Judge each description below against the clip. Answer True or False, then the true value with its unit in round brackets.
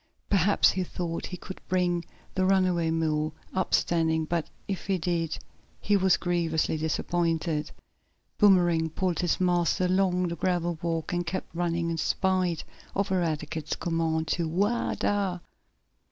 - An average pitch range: False (2.2 semitones)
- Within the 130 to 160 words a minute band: True (140 wpm)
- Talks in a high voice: False (175 Hz)